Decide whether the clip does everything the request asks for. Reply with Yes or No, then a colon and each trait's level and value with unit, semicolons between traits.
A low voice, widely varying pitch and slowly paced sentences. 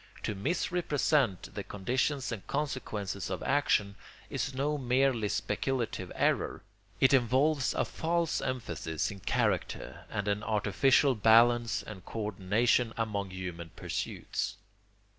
No: low, 115 Hz; average, 5.0 semitones; slow, 120 wpm